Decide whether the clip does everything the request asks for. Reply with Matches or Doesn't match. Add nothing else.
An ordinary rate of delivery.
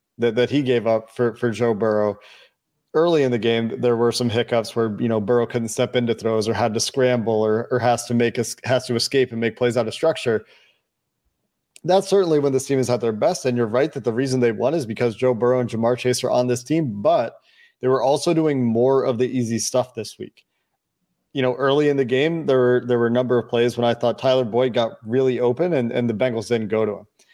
Doesn't match